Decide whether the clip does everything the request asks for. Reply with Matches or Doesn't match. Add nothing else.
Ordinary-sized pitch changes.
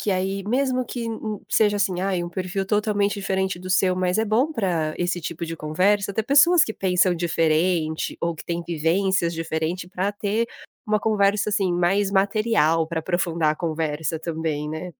Matches